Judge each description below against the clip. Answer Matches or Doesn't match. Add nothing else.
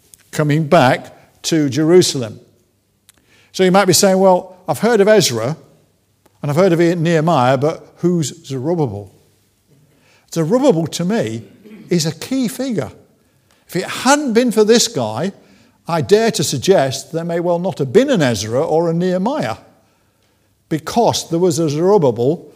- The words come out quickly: Doesn't match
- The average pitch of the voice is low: Doesn't match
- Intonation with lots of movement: Matches